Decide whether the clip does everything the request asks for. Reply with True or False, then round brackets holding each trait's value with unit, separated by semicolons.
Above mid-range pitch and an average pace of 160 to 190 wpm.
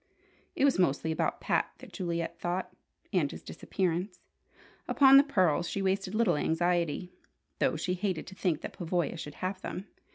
False (180 Hz; 165 wpm)